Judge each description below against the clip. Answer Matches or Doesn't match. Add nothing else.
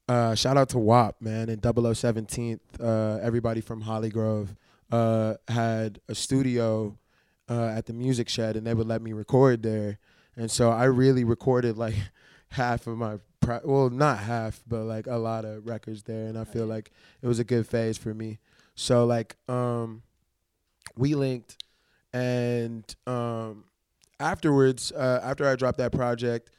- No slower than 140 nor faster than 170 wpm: Matches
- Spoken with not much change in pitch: Matches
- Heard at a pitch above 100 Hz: Matches